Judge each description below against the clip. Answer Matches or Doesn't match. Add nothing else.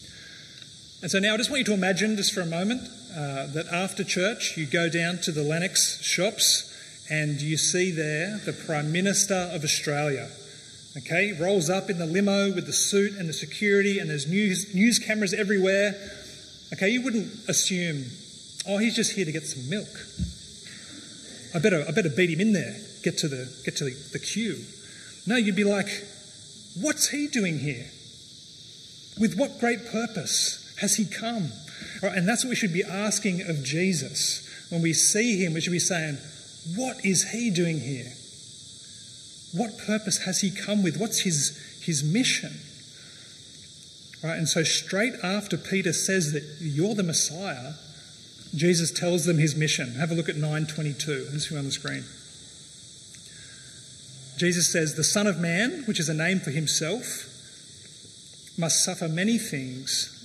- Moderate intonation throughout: Matches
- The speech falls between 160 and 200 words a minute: Matches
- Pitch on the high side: Doesn't match